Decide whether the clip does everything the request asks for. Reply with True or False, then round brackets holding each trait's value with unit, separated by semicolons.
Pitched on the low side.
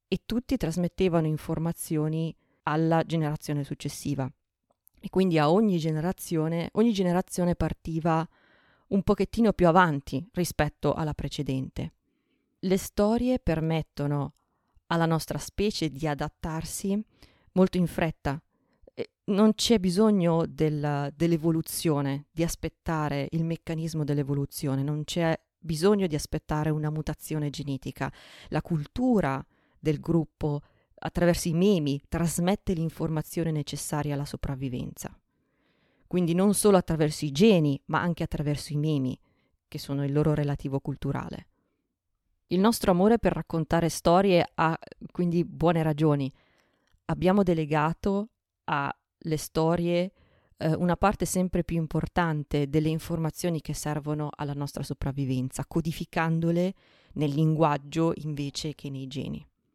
False (160 Hz)